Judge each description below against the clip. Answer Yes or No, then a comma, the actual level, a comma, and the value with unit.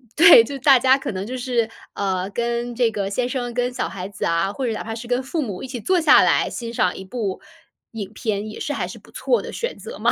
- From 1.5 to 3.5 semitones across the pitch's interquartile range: No, average, 4.2 semitones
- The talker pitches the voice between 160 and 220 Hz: No, high, 235 Hz